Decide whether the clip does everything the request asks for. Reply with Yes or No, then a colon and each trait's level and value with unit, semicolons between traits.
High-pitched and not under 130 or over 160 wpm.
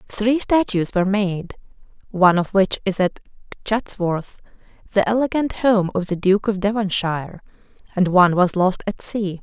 Yes: high, 195 Hz; average, 155 wpm